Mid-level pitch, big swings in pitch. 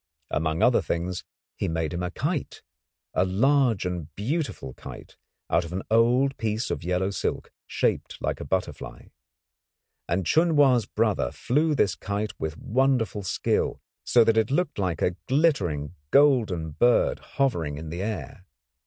No: low, 100 Hz; wide, 7.3 semitones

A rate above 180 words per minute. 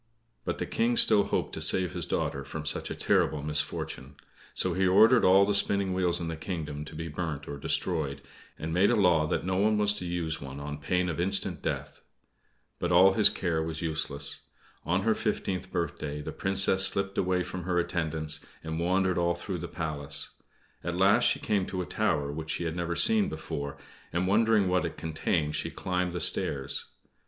Yes: average, 200 wpm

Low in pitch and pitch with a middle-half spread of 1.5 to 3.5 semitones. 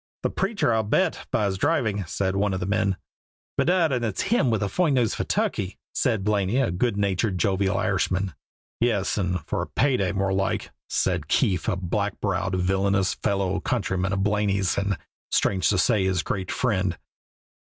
Yes: low, 100 Hz; average, 2.7 semitones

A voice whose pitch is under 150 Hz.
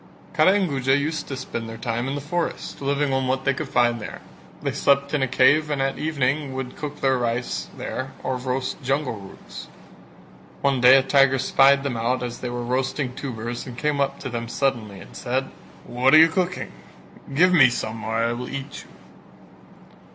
Yes: low, 135 Hz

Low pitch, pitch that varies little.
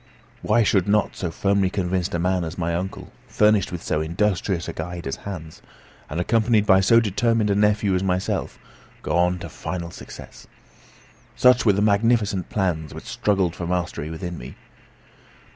No: very low, 95 Hz; average, 3.1 semitones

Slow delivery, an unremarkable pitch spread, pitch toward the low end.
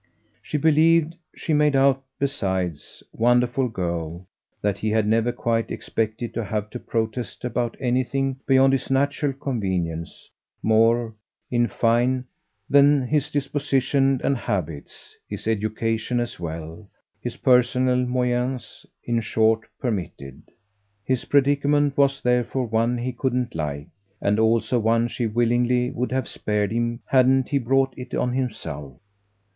Yes: slow, 130 wpm; average, 3.3 semitones; low, 120 Hz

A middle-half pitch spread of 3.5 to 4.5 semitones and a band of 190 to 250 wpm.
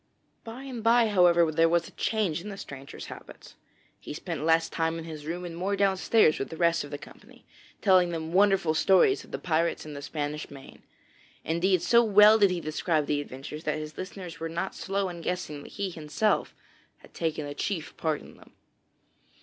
Yes: average, 3.9 semitones; average, 200 wpm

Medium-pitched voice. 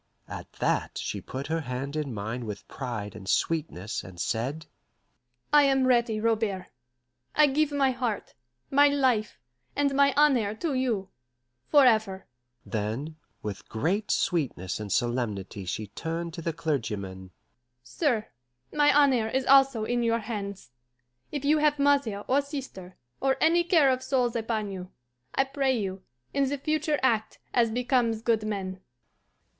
No: high, 220 Hz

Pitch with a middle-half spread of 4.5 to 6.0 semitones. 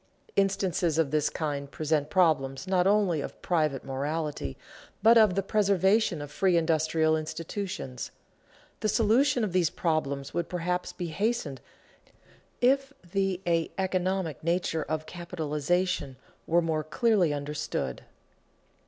No: average, 3.9 semitones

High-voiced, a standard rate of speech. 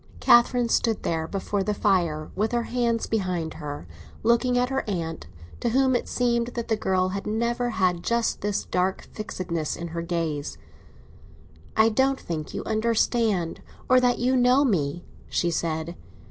Yes: high, 210 Hz; average, 160 wpm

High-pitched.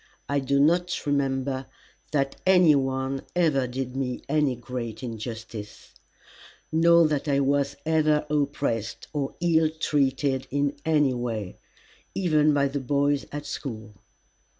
No: medium, 140 Hz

